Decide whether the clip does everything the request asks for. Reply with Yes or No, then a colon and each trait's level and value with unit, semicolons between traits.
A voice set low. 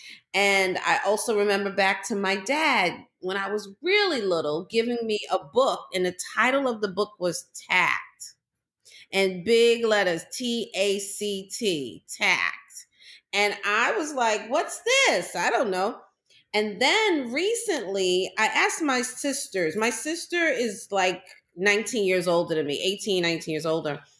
No: high, 205 Hz